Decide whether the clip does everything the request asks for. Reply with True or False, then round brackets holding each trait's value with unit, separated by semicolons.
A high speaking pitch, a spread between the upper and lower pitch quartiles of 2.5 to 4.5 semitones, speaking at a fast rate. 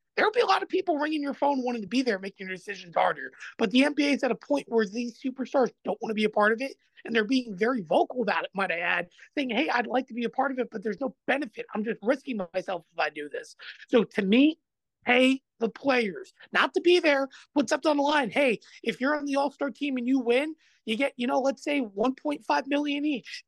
True (260 Hz; 4.0 semitones; 260 wpm)